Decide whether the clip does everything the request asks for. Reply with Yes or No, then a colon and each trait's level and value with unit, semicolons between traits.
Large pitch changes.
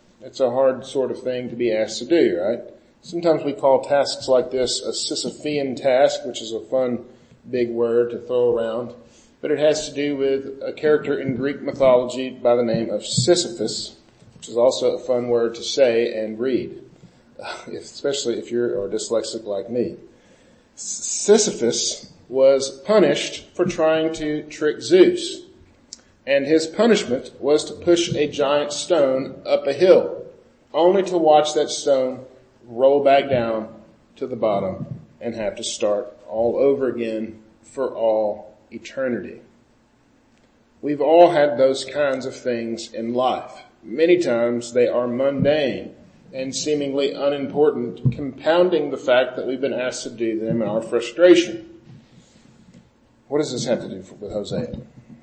No: average, 4.7 semitones